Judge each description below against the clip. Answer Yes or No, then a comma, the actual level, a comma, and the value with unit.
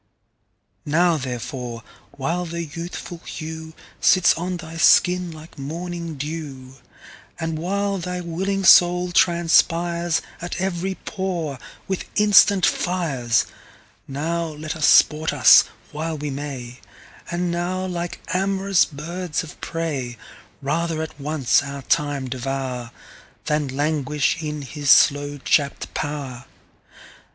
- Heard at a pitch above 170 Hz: No, medium, 160 Hz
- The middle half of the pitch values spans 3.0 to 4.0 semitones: Yes, average, 3.6 semitones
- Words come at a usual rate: No, slow, 100 wpm